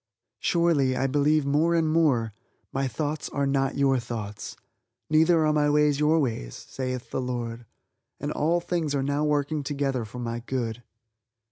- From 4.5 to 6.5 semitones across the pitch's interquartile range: No, average, 3.3 semitones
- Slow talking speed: No, average, 160 wpm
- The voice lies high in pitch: No, medium, 140 Hz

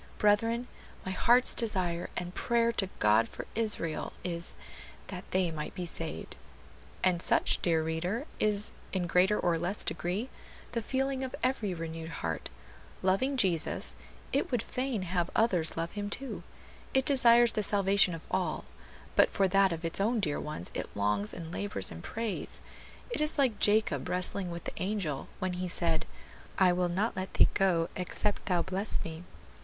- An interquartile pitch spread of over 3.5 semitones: Yes, average, 4.4 semitones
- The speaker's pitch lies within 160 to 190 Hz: Yes, medium, 185 Hz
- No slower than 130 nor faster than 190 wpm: Yes, average, 170 wpm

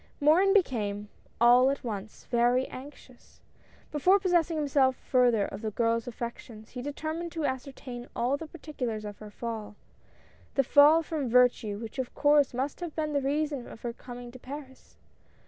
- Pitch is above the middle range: Yes, very high, 255 Hz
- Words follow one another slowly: No, average, 175 wpm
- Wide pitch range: No, average, 3.9 semitones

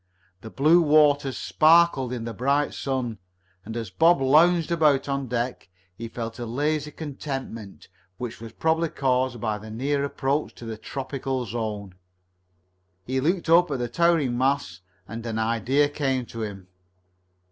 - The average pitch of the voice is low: Yes, low, 130 Hz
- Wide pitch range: No, average, 4.2 semitones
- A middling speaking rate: Yes, average, 155 wpm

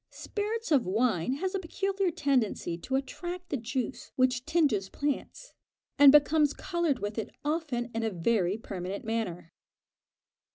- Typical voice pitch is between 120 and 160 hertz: No, very high, 265 Hz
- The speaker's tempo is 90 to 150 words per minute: Yes, average, 140 wpm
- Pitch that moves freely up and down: Yes, wide, 6.6 semitones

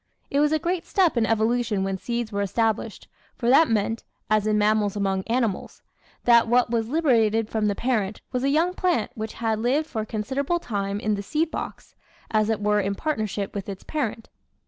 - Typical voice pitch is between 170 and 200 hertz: No, high, 225 Hz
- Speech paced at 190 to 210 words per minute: Yes, fast, 205 wpm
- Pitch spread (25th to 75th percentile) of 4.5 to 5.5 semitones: No, average, 3.7 semitones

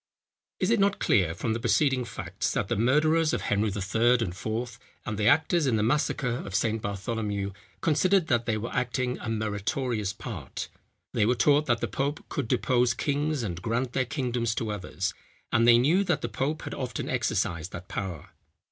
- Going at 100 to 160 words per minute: No, average, 190 wpm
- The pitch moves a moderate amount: Yes, average, 4.3 semitones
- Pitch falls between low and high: No, low, 120 Hz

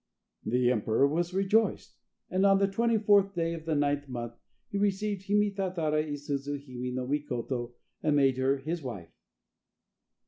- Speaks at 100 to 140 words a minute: No, average, 160 wpm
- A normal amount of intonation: No, wide, 6.8 semitones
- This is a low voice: No, medium, 150 Hz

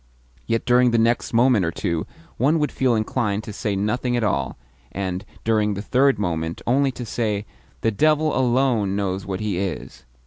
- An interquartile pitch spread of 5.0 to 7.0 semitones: No, average, 4.0 semitones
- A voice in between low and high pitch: No, low, 110 Hz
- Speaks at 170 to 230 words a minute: Yes, average, 180 wpm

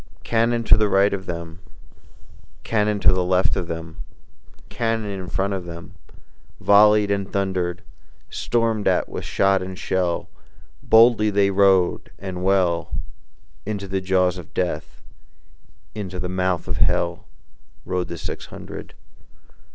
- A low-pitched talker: Yes, very low, 95 Hz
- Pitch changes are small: Yes, narrow, 2.2 semitones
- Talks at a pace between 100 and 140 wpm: Yes, slow, 135 wpm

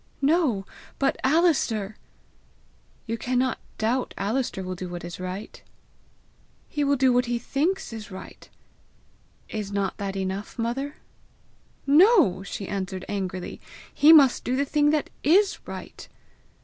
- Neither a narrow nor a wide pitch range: No, wide, 6.5 semitones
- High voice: Yes, high, 240 Hz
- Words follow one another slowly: Yes, slow, 130 wpm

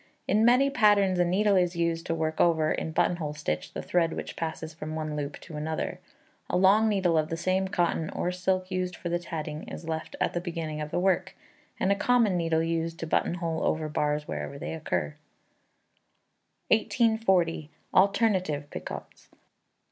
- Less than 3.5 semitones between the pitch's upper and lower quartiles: Yes, average, 3.0 semitones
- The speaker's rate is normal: Yes, average, 175 wpm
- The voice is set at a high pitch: No, medium, 170 Hz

